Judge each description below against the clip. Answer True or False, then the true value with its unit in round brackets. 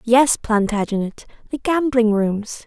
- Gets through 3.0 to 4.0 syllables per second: True (3.9 syllables/s)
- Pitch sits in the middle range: False (230 Hz)